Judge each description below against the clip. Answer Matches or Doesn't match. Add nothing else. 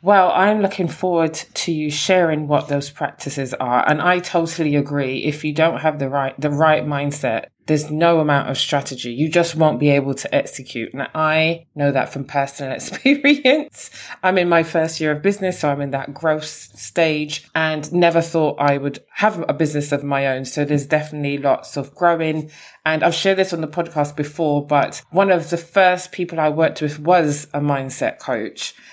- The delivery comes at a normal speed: Matches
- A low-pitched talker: Doesn't match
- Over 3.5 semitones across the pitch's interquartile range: Doesn't match